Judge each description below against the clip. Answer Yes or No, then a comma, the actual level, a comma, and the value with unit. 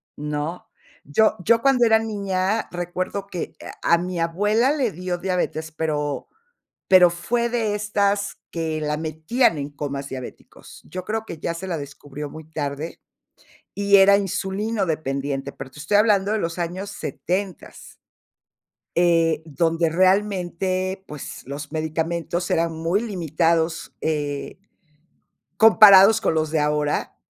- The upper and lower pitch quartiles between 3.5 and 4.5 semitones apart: Yes, average, 4.2 semitones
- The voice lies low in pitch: No, medium, 175 Hz